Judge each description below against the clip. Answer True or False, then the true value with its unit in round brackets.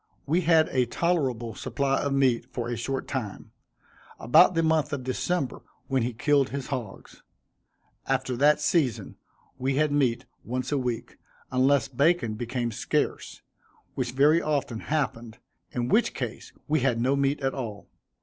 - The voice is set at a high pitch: False (135 Hz)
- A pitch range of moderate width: True (3.3 semitones)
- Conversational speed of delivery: True (155 wpm)